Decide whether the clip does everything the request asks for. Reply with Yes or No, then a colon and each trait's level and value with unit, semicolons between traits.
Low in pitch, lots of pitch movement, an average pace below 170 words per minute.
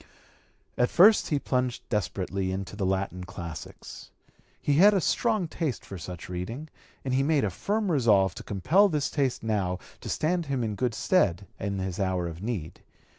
No: low, 110 Hz; wide, 8.3 semitones; average, 175 wpm